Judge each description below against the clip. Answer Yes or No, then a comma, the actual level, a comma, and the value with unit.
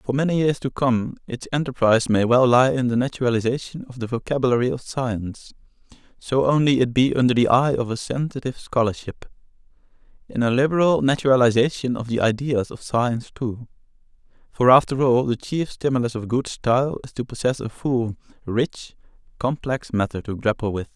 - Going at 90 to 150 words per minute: No, average, 165 wpm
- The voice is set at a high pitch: No, low, 125 Hz